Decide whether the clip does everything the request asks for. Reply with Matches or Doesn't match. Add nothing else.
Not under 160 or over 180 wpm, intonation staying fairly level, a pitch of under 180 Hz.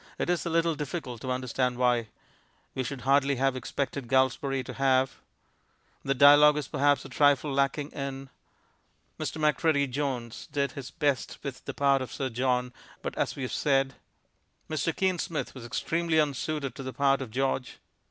Matches